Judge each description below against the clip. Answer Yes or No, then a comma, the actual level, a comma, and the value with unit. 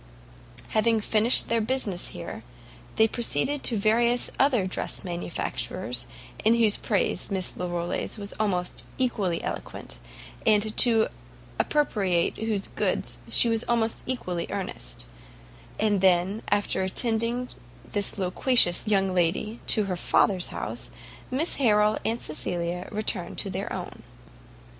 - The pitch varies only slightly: No, average, 4.0 semitones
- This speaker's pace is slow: Yes, slow, 125 wpm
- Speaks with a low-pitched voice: No, high, 210 Hz